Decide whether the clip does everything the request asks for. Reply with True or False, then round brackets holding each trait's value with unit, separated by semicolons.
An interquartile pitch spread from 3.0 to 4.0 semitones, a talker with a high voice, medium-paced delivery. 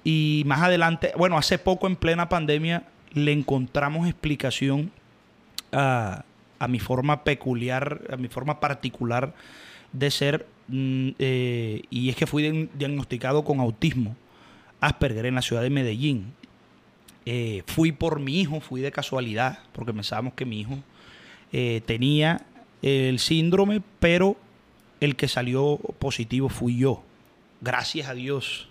False (3.7 semitones; 140 Hz; 135 wpm)